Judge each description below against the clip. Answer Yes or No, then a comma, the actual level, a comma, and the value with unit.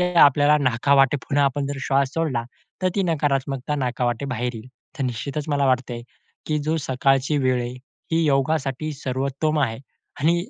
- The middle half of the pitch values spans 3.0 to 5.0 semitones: No, narrow, 2.6 semitones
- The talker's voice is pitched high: No, medium, 140 Hz